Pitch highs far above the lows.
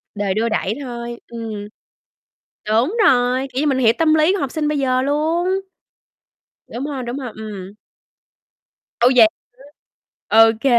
No: average, 4.2 semitones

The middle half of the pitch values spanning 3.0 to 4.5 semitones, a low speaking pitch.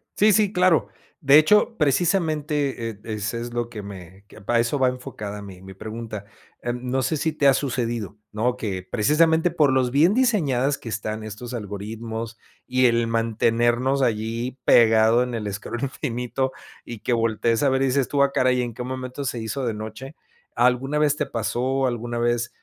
Yes: average, 3.3 semitones; low, 120 Hz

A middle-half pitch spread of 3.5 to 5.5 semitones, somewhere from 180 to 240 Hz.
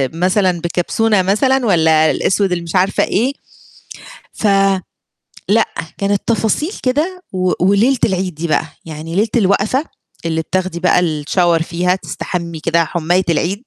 Yes: average, 3.8 semitones; medium, 185 Hz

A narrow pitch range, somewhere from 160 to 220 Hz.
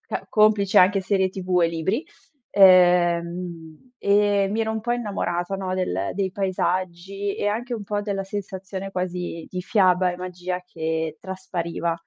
Yes: narrow, 2.3 semitones; medium, 185 Hz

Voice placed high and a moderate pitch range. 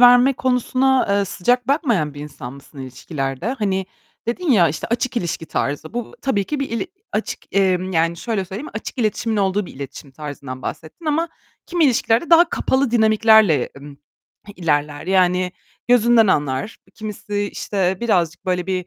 No: high, 195 Hz; wide, 6.9 semitones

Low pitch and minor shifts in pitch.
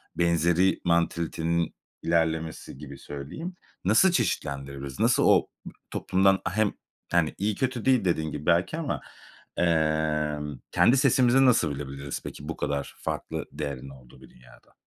No: very low, 80 Hz; average, 5.2 semitones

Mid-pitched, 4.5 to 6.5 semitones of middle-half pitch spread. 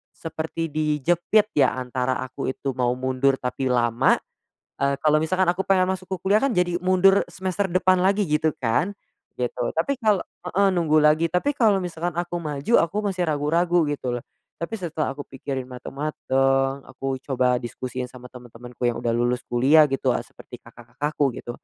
Yes: medium, 150 Hz; wide, 5.6 semitones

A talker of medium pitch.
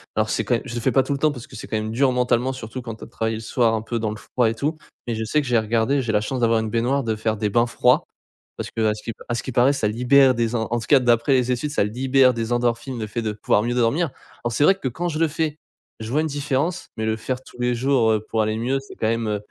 No: low, 120 Hz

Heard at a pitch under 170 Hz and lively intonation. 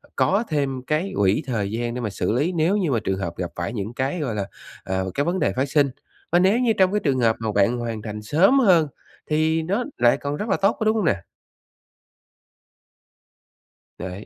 Yes: medium, 140 Hz; wide, 8.5 semitones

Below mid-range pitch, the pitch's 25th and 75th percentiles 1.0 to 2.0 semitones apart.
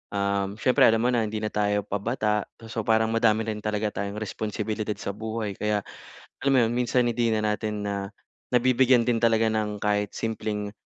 Yes: low, 110 Hz; narrow, 1.6 semitones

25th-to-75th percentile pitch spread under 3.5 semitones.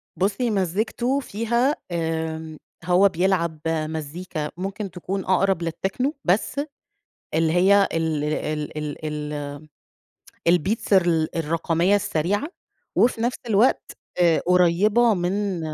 No: average, 3.9 semitones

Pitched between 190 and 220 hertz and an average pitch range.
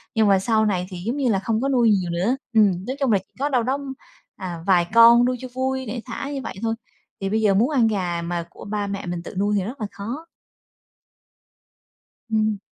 Yes: high, 215 Hz; average, 4.1 semitones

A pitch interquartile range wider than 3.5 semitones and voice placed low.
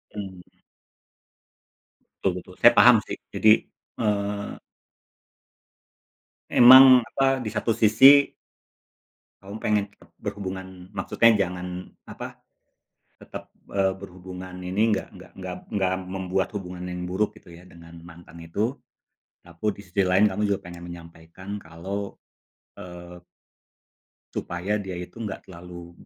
No: average, 2.7 semitones; very low, 95 Hz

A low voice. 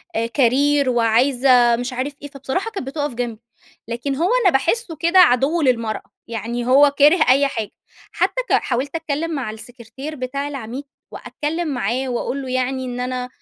No: very high, 265 Hz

